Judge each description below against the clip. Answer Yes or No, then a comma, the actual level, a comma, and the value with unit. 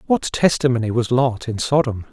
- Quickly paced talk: No, average, 170 wpm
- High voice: No, low, 125 Hz